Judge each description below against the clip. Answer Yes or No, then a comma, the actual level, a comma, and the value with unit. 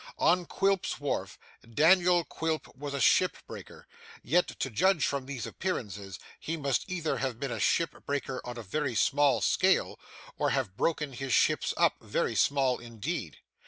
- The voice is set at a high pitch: No, medium, 140 Hz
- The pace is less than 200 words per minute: Yes, average, 160 wpm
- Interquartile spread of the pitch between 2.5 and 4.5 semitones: No, average, 5.3 semitones